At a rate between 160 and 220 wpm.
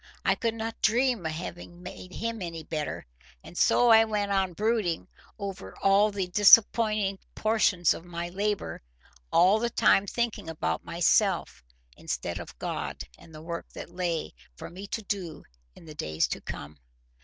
Yes: average, 165 wpm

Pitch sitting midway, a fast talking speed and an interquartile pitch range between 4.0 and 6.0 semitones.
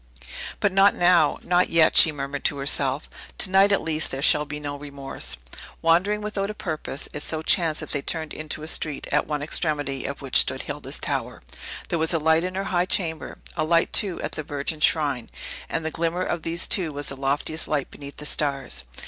No: medium, 155 Hz; fast, 210 wpm; average, 3.2 semitones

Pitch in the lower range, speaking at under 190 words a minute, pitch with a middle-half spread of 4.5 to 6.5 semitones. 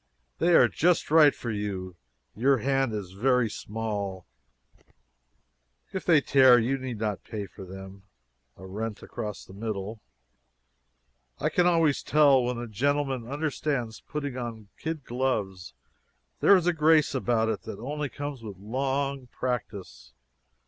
Yes: low, 120 Hz; average, 145 wpm; average, 5.3 semitones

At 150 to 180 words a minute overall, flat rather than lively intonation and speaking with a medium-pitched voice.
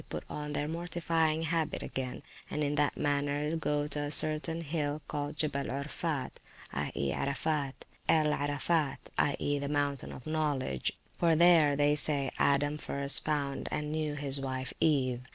Yes: average, 155 wpm; narrow, 1.8 semitones; medium, 145 Hz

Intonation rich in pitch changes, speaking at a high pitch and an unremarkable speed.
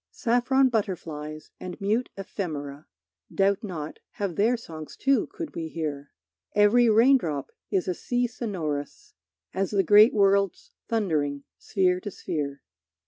No: wide, 6.3 semitones; high, 195 Hz; slow, 130 wpm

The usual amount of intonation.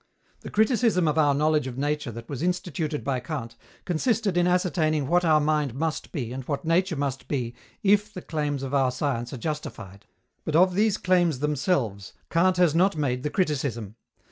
Yes: average, 5.0 semitones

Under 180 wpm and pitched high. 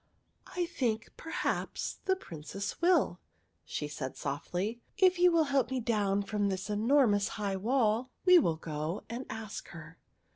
Yes: average, 160 wpm; high, 215 Hz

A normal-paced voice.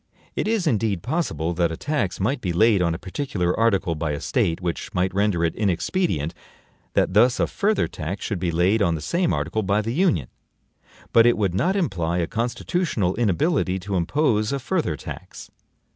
Yes: average, 190 wpm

